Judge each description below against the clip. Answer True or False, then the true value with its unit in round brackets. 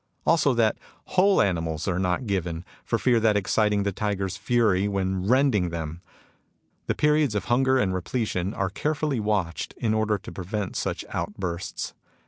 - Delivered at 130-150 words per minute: False (160 wpm)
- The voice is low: True (105 Hz)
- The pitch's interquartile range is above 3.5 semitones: True (4.4 semitones)